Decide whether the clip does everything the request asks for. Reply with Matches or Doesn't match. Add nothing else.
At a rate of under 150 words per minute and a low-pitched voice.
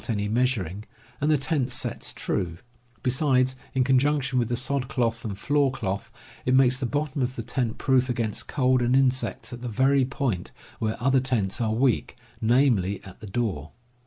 Doesn't match